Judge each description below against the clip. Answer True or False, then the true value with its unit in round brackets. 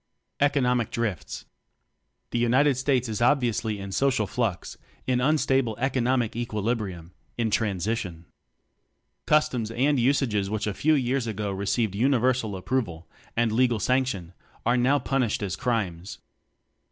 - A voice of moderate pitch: False (120 Hz)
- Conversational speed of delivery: False (130 wpm)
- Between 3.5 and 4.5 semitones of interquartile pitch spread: True (3.9 semitones)